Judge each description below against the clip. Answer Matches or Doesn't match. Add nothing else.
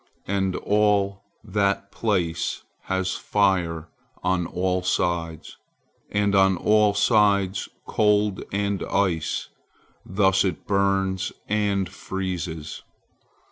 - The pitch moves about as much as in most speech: Doesn't match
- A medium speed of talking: Doesn't match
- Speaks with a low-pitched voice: Matches